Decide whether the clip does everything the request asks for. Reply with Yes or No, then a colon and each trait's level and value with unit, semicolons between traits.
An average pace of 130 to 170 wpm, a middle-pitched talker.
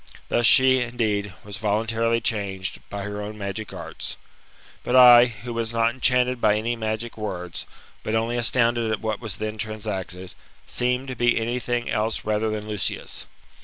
No: average, 165 wpm; low, 110 Hz